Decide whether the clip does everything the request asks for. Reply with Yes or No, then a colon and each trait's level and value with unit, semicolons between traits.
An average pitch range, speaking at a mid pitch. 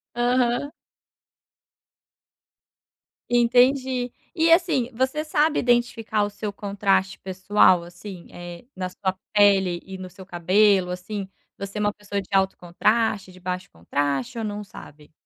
No: average, 4.6 semitones; high, 205 Hz